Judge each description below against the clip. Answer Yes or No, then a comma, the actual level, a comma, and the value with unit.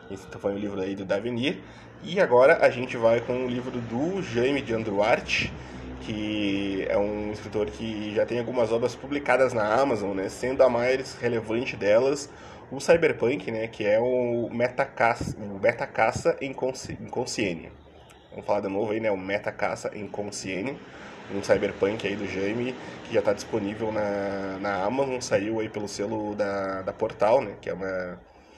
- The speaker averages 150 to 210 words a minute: Yes, average, 175 wpm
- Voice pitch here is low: Yes, low, 110 Hz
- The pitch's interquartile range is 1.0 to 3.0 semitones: No, average, 3.8 semitones